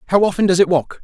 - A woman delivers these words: No, male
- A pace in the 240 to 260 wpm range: No, fast, 290 wpm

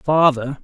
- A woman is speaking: No, male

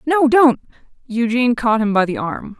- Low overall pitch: No, high, 240 Hz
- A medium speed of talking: Yes, average, 185 wpm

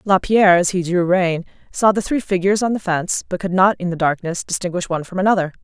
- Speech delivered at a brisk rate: Yes, fast, 235 wpm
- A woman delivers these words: Yes, female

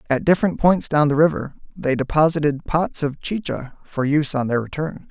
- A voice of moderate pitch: Yes, medium, 150 Hz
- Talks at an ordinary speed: Yes, average, 190 wpm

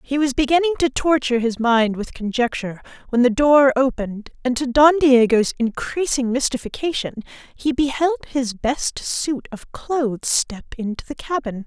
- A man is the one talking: No, female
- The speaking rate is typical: Yes, average, 155 wpm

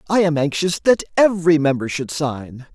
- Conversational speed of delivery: Yes, average, 175 wpm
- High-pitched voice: No, medium, 160 Hz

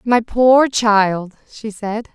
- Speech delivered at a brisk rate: No, average, 140 wpm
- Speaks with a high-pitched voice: Yes, high, 220 Hz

